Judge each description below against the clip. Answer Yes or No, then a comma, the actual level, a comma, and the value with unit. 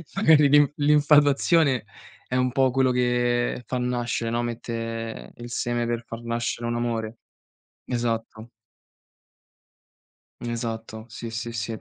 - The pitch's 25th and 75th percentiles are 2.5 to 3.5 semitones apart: No, narrow, 1.8 semitones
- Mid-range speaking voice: No, low, 120 Hz